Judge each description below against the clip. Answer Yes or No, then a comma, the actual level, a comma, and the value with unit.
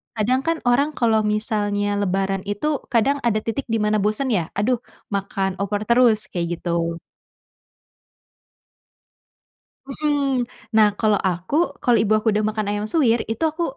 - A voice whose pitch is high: Yes, high, 215 Hz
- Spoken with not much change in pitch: No, average, 3.5 semitones